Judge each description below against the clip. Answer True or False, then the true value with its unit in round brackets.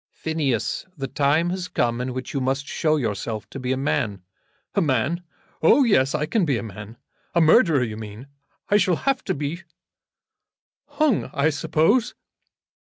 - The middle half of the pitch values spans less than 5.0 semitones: False (5.4 semitones)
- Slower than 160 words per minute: False (170 wpm)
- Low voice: False (145 Hz)